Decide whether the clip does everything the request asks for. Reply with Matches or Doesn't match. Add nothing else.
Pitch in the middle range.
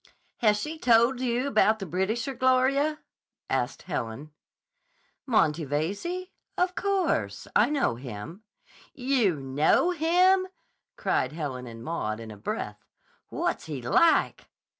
Doesn't match